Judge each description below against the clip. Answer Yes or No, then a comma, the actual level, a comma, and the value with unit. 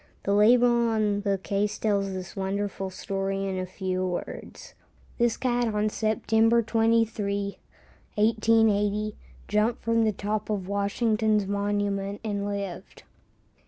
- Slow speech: Yes, slow, 125 wpm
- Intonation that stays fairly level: Yes, narrow, 1.9 semitones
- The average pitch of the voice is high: Yes, high, 205 Hz